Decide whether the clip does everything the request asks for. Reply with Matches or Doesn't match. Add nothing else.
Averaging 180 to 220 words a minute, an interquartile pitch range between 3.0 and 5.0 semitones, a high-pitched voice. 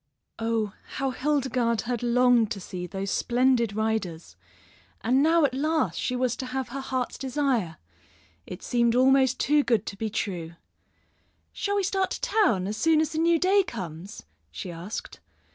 Doesn't match